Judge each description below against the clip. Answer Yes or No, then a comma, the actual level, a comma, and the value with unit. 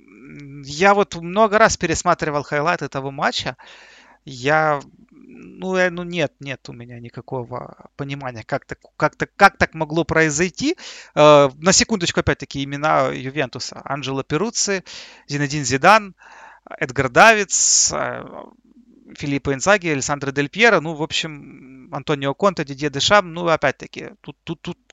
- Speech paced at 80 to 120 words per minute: No, average, 130 wpm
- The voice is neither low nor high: Yes, medium, 155 Hz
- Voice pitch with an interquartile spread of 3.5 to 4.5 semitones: No, wide, 5.4 semitones